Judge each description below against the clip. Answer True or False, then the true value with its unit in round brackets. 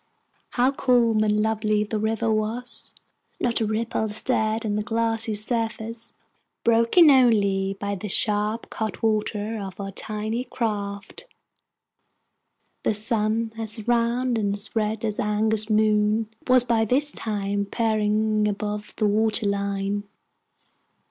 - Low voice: False (215 Hz)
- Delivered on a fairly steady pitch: True (1.5 semitones)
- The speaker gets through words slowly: True (125 wpm)